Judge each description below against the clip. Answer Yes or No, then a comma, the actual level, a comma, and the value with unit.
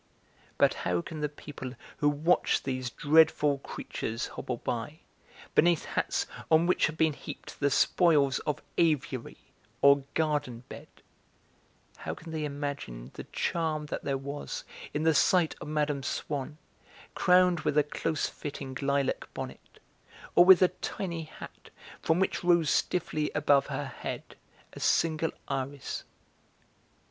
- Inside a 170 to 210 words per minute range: No, average, 140 wpm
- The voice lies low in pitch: No, medium, 150 Hz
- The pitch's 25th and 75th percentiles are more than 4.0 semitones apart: No, narrow, 2.6 semitones